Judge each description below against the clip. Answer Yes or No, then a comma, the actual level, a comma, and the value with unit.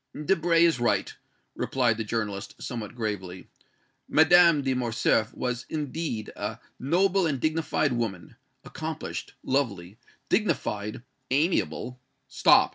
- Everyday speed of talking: No, slow, 115 wpm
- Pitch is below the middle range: Yes, low, 125 Hz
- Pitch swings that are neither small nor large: No, wide, 6.2 semitones